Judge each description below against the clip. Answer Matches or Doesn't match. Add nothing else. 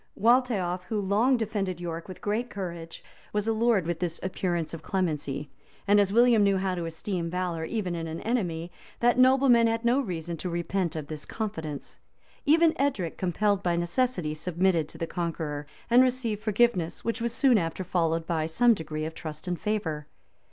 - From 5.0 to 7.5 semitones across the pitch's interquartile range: Matches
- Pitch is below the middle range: Doesn't match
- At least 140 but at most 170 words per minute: Doesn't match